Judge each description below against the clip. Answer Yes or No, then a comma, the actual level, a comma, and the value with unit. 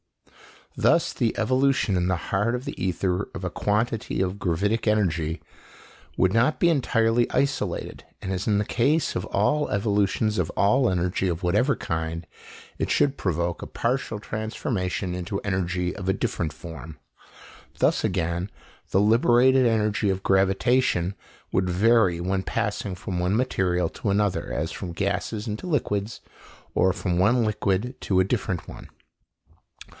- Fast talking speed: No, average, 150 wpm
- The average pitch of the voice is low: Yes, low, 100 Hz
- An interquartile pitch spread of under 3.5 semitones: No, average, 4.0 semitones